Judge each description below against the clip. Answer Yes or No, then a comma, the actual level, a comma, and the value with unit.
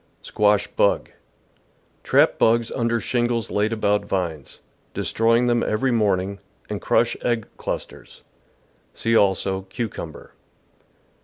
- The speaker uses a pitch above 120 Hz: No, low, 110 Hz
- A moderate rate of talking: No, slow, 110 wpm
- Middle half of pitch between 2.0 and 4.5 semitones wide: Yes, average, 2.9 semitones